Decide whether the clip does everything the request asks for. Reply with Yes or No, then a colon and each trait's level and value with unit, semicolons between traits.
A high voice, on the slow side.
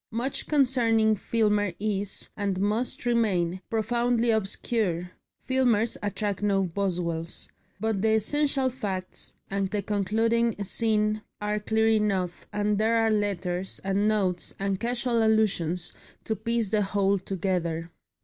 Yes: high, 210 Hz; slow, 125 wpm